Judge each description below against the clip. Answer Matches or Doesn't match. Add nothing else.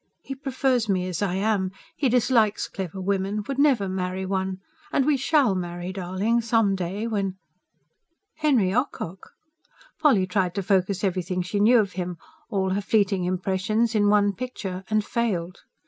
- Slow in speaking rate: Doesn't match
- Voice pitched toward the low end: Doesn't match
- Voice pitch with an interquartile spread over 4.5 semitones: Doesn't match